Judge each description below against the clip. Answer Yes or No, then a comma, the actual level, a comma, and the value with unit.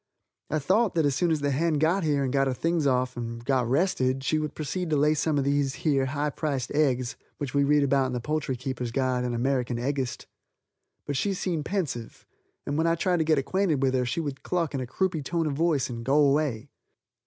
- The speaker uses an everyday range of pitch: Yes, average, 3.3 semitones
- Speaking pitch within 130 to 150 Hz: Yes, medium, 140 Hz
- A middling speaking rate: No, fast, 235 wpm